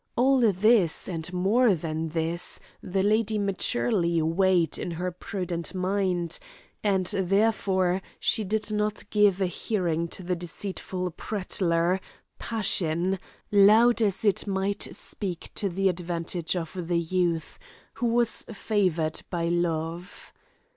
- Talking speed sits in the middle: No, slow, 125 wpm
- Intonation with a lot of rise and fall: No, average, 3.1 semitones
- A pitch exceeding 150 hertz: Yes, medium, 185 Hz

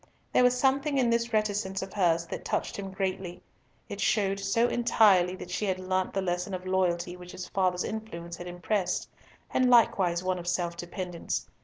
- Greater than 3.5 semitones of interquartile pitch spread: No, average, 3.2 semitones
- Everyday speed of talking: Yes, average, 185 wpm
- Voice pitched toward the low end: No, high, 190 Hz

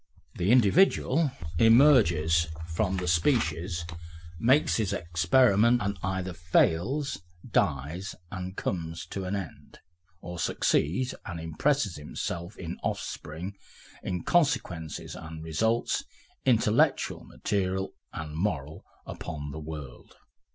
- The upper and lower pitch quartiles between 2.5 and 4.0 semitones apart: No, average, 5.1 semitones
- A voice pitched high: No, very low, 90 Hz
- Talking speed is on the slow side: Yes, slow, 105 wpm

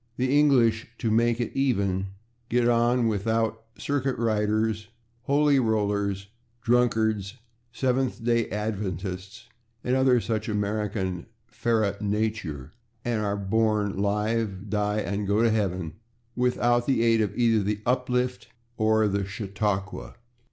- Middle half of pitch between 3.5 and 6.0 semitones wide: No, average, 2.8 semitones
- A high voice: No, low, 110 Hz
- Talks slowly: Yes, slow, 125 wpm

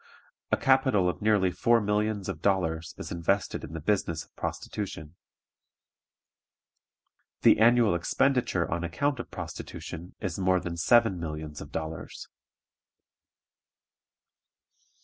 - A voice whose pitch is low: Yes, very low, 95 Hz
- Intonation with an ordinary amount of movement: Yes, average, 4.5 semitones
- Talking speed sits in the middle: No, slow, 115 wpm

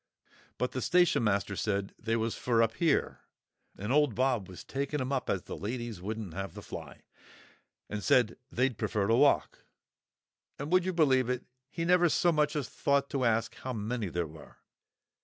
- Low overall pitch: Yes, low, 125 Hz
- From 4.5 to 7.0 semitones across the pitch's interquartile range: Yes, average, 5.0 semitones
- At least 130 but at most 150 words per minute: No, average, 180 wpm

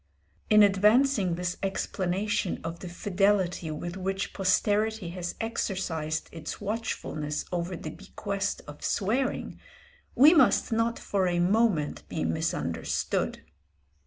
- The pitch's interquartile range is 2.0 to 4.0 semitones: Yes, average, 3.6 semitones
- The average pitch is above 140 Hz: Yes, high, 190 Hz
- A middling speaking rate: No, slow, 115 wpm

